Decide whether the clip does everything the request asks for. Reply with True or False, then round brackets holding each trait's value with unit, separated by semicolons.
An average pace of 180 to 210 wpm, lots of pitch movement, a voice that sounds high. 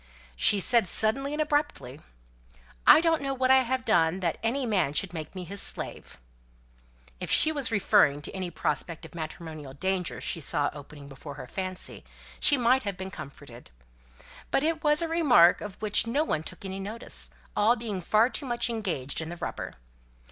True (185 wpm; 7.9 semitones; 200 Hz)